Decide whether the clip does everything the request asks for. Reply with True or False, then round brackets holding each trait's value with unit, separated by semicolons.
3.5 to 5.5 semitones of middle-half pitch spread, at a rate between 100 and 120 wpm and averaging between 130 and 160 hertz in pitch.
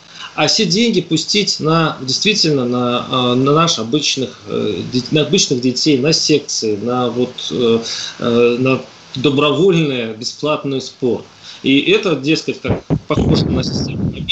True (4.1 semitones; 115 wpm; 140 Hz)